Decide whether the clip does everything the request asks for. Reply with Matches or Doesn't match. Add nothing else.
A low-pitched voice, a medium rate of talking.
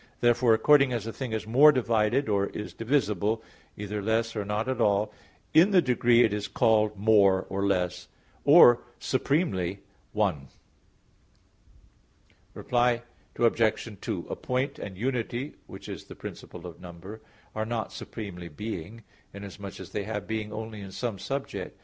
Matches